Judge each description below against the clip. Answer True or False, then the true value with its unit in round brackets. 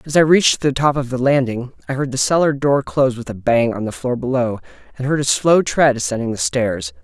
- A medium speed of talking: False (245 wpm)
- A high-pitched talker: False (130 Hz)